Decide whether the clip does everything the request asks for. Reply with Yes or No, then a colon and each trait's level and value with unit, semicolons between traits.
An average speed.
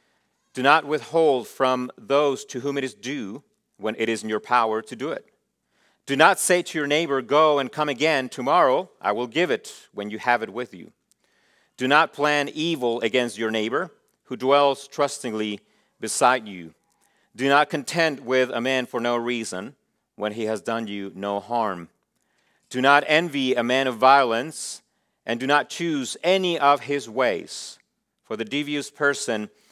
Yes: average, 175 wpm